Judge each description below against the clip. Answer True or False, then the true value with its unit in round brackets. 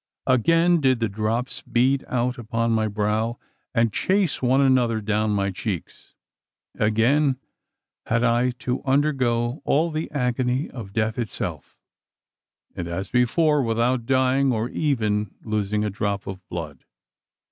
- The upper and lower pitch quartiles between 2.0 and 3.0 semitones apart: False (3.6 semitones)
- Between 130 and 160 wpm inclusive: True (135 wpm)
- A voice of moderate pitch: False (120 Hz)